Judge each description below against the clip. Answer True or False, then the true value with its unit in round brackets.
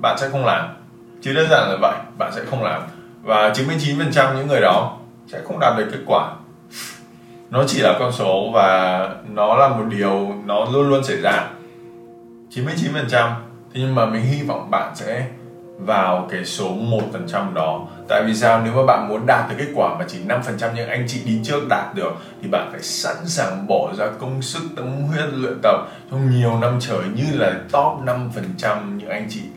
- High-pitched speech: False (120 Hz)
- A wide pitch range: False (3.4 semitones)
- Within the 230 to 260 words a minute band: False (215 wpm)